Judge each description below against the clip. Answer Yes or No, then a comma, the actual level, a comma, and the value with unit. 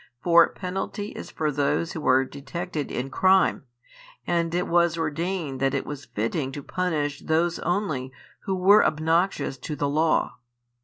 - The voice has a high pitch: No, medium, 160 Hz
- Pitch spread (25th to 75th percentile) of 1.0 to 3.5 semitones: No, average, 3.9 semitones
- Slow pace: No, average, 155 wpm